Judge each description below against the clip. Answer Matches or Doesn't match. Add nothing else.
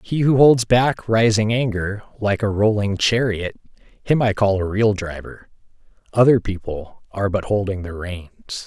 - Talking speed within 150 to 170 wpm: Matches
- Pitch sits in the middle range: Doesn't match